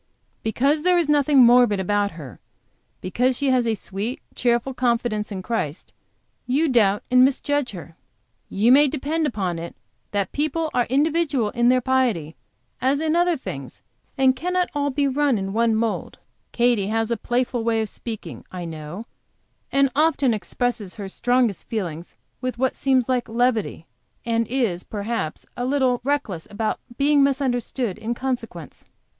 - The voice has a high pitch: Yes, high, 240 Hz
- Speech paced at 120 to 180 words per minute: Yes, average, 155 wpm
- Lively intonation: No, average, 4.5 semitones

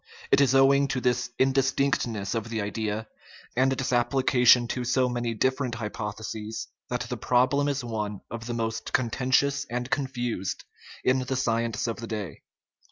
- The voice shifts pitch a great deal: No, average, 2.7 semitones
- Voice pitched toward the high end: No, low, 120 Hz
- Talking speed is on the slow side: No, average, 165 wpm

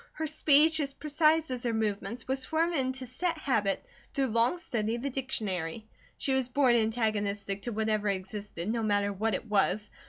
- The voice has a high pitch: Yes, high, 230 Hz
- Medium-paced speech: Yes, average, 180 wpm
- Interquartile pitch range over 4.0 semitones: Yes, average, 4.7 semitones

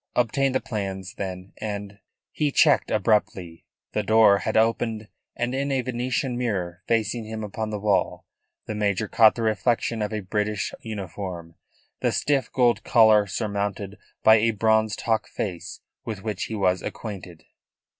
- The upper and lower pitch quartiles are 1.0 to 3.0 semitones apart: Yes, narrow, 2.4 semitones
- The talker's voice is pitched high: No, low, 110 Hz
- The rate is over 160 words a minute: No, average, 155 wpm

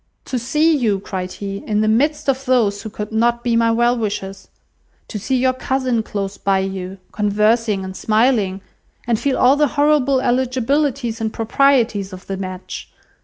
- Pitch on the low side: No, high, 230 Hz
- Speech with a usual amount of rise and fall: Yes, average, 4.4 semitones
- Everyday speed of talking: Yes, average, 170 wpm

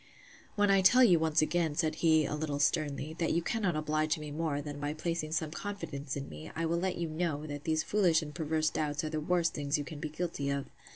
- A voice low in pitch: No, medium, 155 Hz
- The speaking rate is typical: No, fast, 240 wpm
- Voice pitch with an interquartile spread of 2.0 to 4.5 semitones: Yes, narrow, 2.4 semitones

